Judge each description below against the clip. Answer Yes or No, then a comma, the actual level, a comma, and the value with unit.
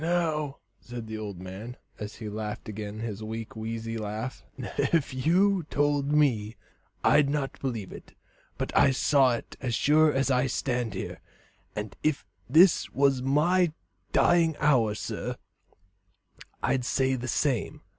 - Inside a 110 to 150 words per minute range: Yes, average, 145 wpm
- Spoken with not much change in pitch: No, average, 5.1 semitones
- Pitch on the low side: Yes, low, 130 Hz